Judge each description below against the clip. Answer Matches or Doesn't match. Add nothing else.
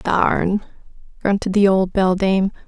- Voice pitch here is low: Doesn't match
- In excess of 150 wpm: Doesn't match